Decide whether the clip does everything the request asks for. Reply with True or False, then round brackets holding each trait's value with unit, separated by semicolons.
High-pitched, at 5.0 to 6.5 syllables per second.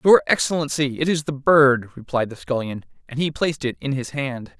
False (140 Hz; 5.3 syllables/s)